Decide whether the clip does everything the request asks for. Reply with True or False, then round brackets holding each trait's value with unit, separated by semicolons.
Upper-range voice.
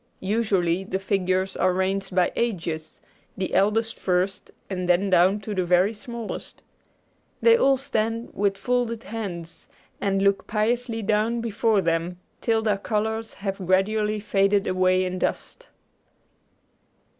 True (200 Hz)